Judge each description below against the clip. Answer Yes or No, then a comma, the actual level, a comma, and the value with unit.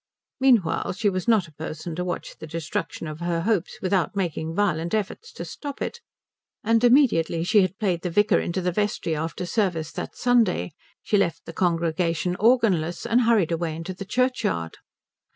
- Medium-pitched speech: Yes, medium, 180 Hz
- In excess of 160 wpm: Yes, average, 175 wpm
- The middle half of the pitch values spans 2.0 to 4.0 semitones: No, average, 4.7 semitones